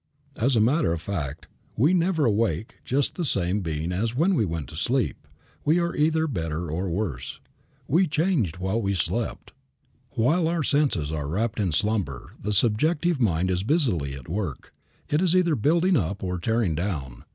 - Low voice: Yes, low, 105 Hz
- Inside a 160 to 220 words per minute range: Yes, average, 175 wpm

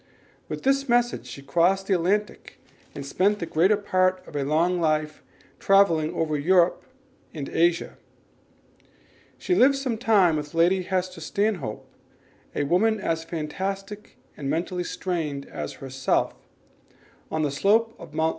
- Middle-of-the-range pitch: Yes, medium, 180 Hz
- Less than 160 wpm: Yes, average, 145 wpm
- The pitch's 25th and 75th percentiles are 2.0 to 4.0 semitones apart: No, average, 4.4 semitones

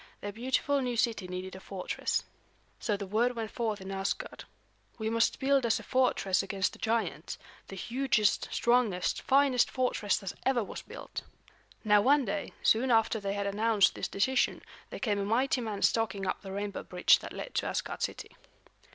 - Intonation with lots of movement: No, average, 3.8 semitones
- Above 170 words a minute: Yes, average, 180 wpm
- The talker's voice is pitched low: No, high, 220 Hz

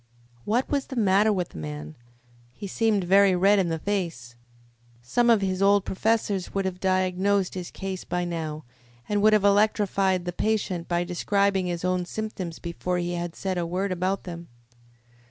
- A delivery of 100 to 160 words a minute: No, average, 175 wpm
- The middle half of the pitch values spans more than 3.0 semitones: No, narrow, 2.5 semitones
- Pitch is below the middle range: No, medium, 185 Hz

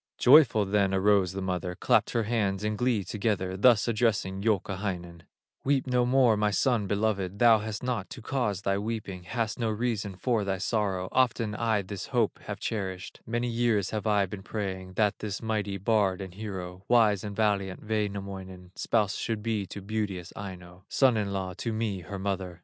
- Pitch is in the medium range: No, low, 105 Hz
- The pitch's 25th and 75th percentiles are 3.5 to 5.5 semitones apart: No, average, 2.7 semitones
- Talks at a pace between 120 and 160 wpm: No, average, 180 wpm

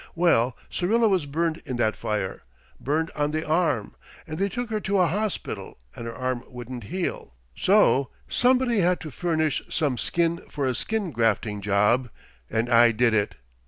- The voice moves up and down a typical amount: No, wide, 7.2 semitones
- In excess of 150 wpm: Yes, average, 170 wpm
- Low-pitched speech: No, medium, 150 Hz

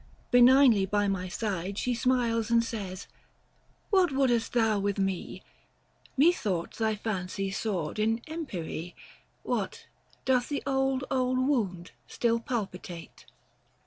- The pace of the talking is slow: Yes, slow, 120 wpm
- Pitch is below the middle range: No, high, 225 Hz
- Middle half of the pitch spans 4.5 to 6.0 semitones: Yes, average, 4.8 semitones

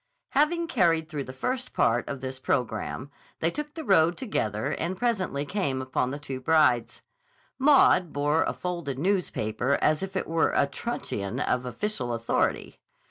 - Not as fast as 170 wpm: Yes, average, 160 wpm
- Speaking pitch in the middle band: Yes, medium, 155 Hz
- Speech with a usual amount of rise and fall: No, wide, 6.8 semitones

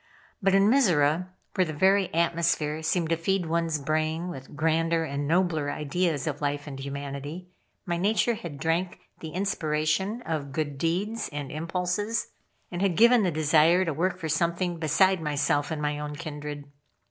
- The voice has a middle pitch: Yes, medium, 165 Hz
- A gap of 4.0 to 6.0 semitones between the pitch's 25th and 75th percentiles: No, average, 3.5 semitones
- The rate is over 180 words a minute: No, average, 165 wpm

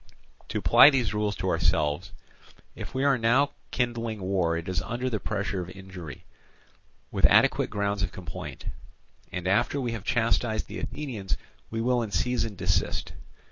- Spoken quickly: No, average, 160 wpm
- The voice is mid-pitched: No, low, 105 Hz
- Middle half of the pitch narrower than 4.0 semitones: No, average, 4.4 semitones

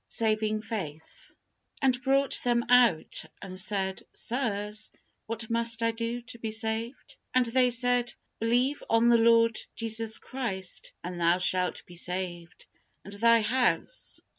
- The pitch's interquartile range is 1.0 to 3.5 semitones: Yes, average, 3.0 semitones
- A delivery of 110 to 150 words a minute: Yes, average, 140 wpm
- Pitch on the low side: No, high, 230 Hz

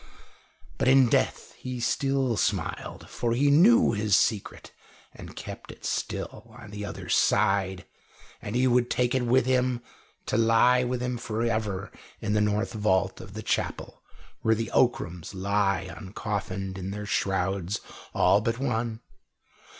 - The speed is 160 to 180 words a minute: No, average, 150 wpm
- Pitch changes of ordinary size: Yes, average, 3.8 semitones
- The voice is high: No, low, 110 Hz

